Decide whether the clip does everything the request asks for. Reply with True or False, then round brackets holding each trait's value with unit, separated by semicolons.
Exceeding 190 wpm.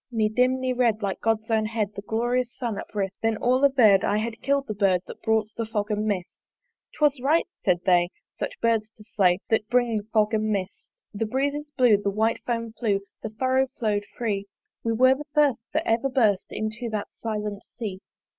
True (200 wpm)